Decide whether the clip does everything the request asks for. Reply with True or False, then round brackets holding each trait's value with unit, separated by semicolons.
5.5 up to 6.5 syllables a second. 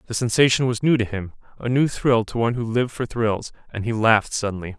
True (6.2 syllables/s)